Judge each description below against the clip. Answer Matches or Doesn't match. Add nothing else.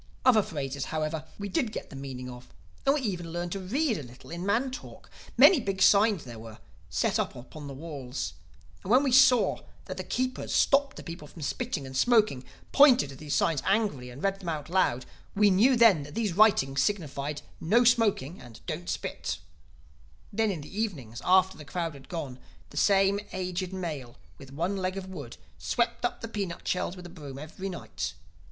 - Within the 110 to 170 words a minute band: Doesn't match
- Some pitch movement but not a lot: Doesn't match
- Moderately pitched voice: Matches